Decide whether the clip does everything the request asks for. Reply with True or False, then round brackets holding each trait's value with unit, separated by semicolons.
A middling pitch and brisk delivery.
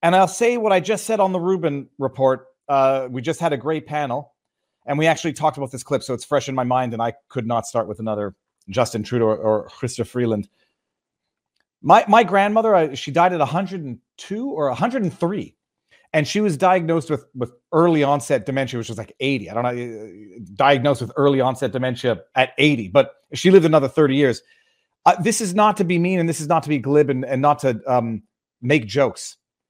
True (145 Hz; 210 wpm)